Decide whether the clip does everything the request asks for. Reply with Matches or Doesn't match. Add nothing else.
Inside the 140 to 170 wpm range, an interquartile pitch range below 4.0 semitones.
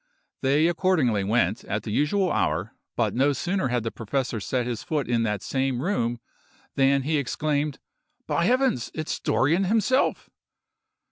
Doesn't match